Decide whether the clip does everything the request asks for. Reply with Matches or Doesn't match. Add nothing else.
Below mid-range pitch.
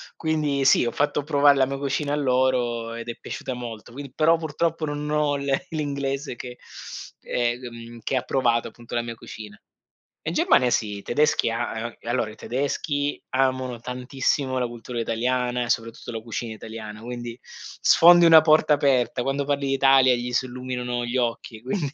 Matches